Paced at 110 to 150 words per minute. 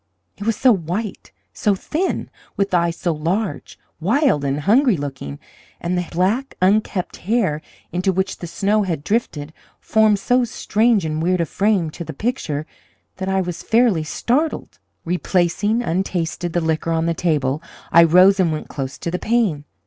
No: average, 165 wpm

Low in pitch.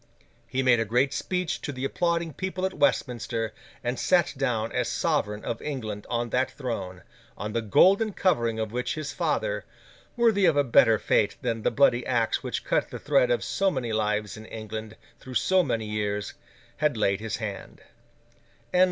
Yes: low, 120 Hz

